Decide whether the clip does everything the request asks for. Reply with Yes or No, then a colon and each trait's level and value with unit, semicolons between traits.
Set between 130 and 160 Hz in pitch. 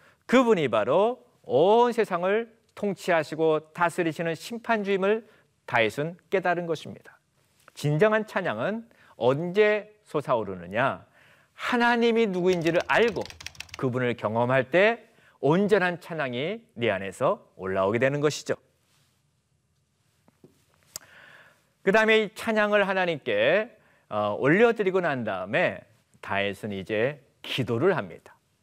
No: medium, 185 Hz